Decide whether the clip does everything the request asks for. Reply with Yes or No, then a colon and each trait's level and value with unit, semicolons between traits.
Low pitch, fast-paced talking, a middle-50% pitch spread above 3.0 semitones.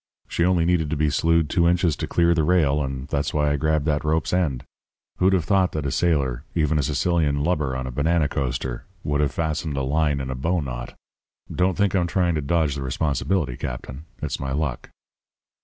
Yes: very low, 75 Hz; fast, 210 wpm; average, 3.6 semitones